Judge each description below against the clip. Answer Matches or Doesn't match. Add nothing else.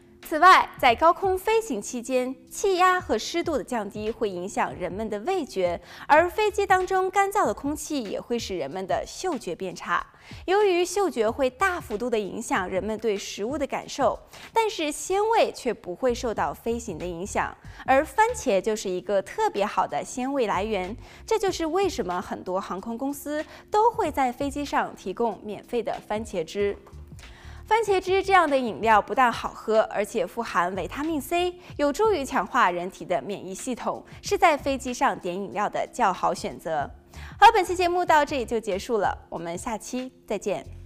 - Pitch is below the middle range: Doesn't match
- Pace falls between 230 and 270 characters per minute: Matches